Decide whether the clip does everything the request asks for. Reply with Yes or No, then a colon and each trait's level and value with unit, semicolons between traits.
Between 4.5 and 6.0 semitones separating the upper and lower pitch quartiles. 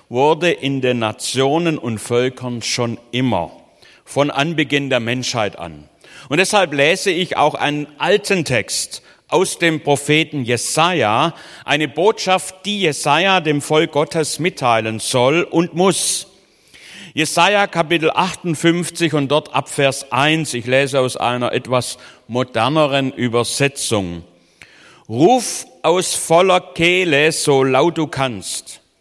Yes: average, 5.0 semitones